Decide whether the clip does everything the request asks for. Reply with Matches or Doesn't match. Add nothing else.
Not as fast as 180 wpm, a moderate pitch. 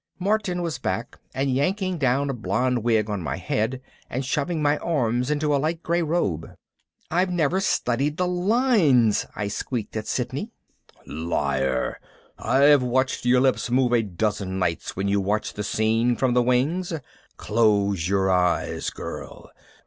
Doesn't match